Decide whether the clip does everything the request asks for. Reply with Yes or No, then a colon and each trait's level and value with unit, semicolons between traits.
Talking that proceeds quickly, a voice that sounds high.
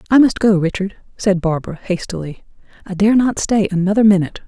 No: average, 175 wpm; high, 195 Hz